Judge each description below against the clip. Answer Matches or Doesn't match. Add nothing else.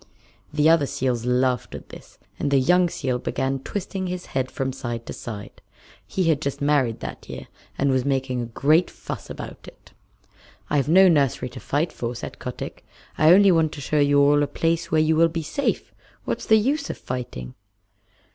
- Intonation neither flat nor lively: Matches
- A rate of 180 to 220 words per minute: Matches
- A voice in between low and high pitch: Matches